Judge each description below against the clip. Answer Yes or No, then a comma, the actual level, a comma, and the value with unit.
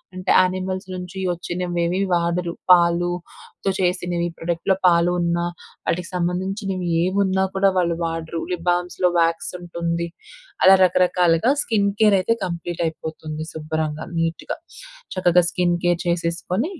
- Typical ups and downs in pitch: No, narrow, 1.4 semitones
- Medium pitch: Yes, medium, 175 Hz